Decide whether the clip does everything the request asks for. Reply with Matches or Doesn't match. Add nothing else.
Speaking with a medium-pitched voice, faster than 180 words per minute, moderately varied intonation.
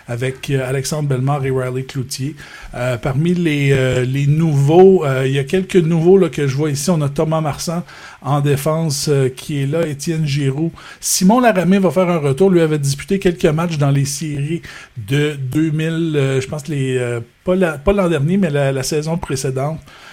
Matches